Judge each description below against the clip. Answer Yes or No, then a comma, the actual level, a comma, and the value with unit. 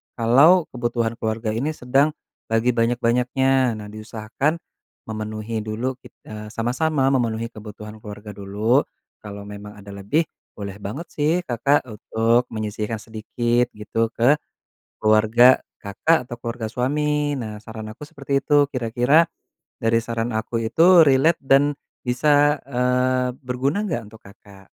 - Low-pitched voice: Yes, low, 120 Hz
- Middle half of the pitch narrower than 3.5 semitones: No, average, 3.8 semitones